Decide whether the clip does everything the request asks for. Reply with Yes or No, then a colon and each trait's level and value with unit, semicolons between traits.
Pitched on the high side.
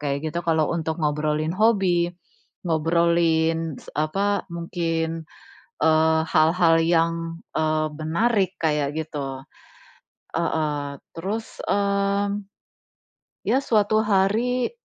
No: medium, 165 Hz